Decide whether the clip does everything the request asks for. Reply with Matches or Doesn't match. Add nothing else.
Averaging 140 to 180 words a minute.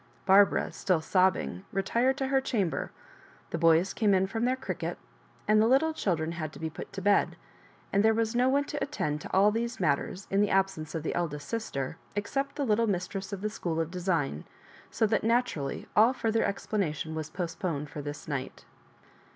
Doesn't match